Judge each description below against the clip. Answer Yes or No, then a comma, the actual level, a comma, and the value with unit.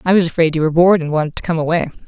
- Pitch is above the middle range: No, medium, 165 Hz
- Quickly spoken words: Yes, fast, 320 wpm